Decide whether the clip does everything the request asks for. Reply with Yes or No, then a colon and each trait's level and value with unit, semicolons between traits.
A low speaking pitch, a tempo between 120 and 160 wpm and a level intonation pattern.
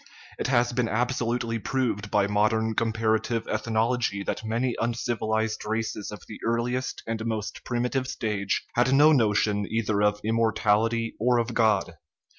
Yes: low, 115 Hz; average, 140 wpm; narrow, 1.9 semitones